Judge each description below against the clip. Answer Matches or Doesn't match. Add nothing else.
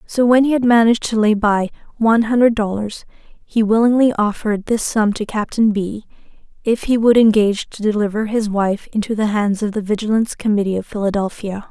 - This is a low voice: Doesn't match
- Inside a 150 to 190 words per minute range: Matches